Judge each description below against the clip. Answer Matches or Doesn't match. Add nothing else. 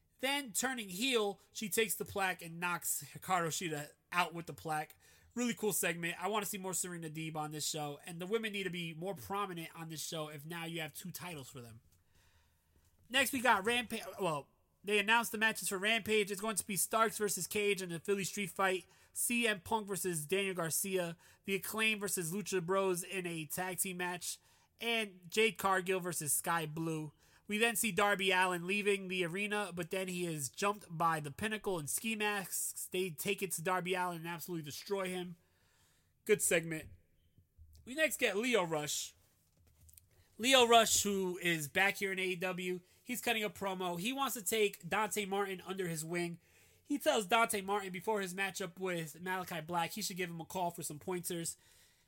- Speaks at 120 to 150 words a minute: Doesn't match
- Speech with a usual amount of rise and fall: Matches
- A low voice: Doesn't match